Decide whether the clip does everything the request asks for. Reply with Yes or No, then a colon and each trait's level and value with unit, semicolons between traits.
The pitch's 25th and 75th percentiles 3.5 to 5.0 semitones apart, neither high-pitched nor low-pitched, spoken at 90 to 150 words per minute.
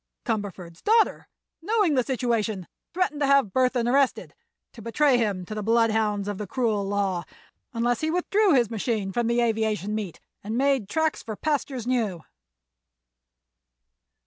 No: average, 4.7 semitones; high, 230 Hz; average, 140 wpm